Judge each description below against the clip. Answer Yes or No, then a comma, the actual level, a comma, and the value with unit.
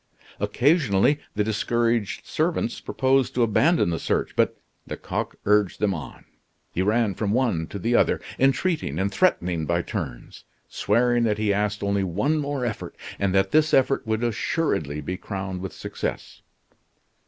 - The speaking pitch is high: No, low, 105 Hz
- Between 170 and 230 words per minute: No, average, 155 wpm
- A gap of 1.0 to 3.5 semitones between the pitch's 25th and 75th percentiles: No, average, 4.6 semitones